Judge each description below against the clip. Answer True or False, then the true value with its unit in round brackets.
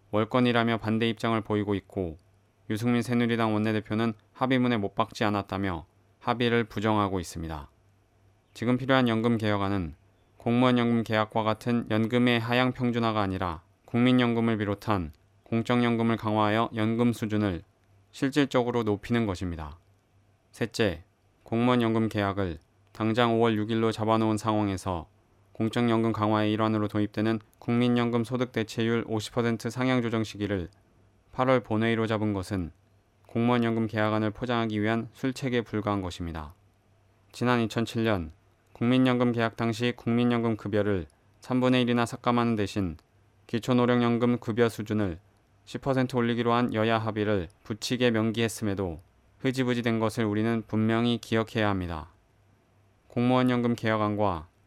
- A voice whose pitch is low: True (110 Hz)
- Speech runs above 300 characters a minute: True (320 characters per minute)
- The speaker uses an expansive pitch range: False (2.7 semitones)